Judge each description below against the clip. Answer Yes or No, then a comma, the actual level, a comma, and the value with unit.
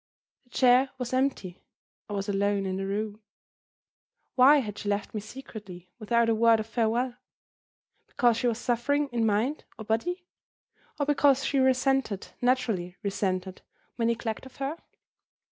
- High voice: Yes, high, 230 Hz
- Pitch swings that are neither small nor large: Yes, average, 4.2 semitones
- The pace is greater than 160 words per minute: No, average, 150 wpm